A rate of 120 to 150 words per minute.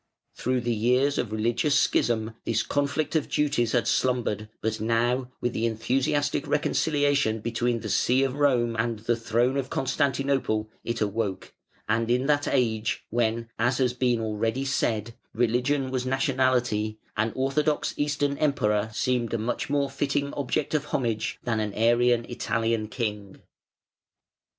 Yes: average, 145 wpm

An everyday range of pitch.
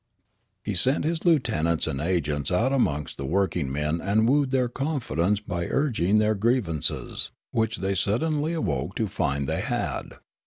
No: wide, 7.5 semitones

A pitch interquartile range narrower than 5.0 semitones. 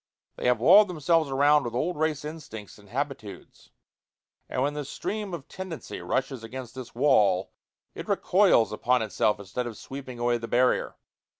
Yes: average, 4.4 semitones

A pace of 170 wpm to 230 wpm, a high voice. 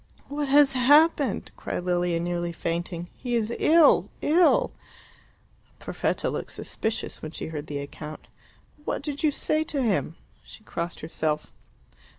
No: average, 140 wpm; high, 205 Hz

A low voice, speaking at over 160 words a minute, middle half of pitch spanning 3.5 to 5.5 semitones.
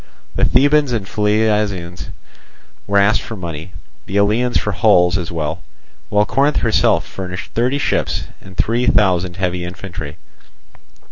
No: low, 100 Hz; slow, 135 wpm; average, 3.8 semitones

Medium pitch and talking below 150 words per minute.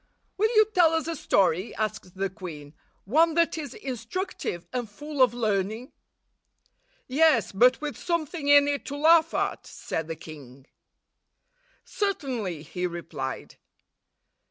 No: high, 245 Hz; slow, 135 wpm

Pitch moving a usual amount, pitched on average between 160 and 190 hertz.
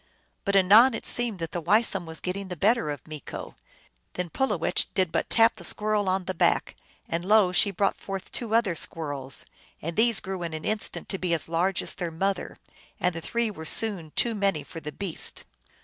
Yes: average, 4.2 semitones; medium, 185 Hz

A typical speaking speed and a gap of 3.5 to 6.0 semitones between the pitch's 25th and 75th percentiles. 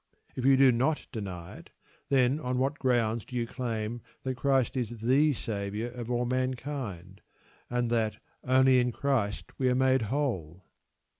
No: average, 160 wpm; average, 2.9 semitones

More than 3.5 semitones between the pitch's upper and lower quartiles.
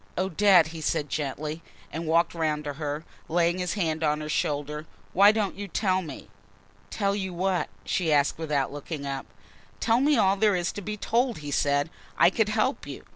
Yes: average, 4.7 semitones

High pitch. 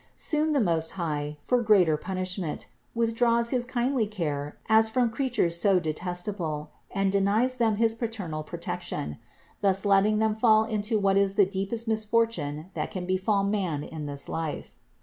Yes: high, 200 Hz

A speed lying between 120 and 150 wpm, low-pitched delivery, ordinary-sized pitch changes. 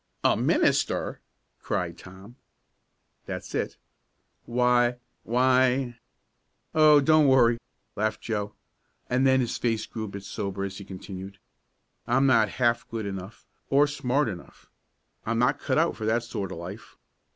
Yes: average, 145 wpm; low, 120 Hz; average, 4.4 semitones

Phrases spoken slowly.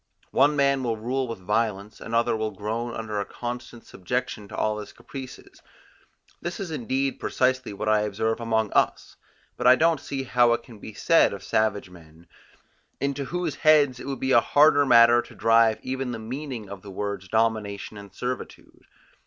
No: average, 180 wpm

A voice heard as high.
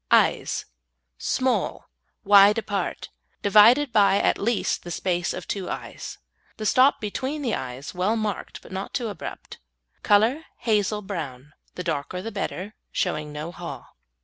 Yes: high, 205 Hz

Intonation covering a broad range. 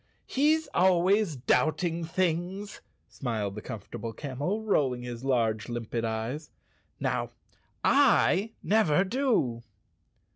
Yes: wide, 8.8 semitones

